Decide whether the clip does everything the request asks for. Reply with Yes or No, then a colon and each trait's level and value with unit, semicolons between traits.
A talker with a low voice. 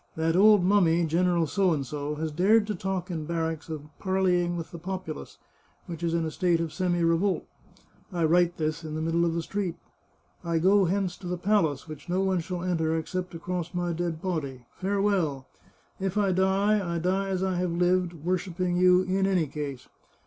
No: medium, 175 Hz